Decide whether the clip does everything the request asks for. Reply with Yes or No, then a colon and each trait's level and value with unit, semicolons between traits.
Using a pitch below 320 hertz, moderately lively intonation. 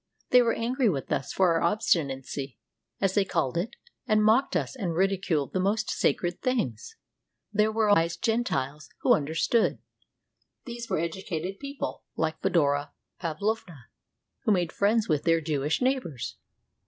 No: medium, 185 Hz; wide, 5.8 semitones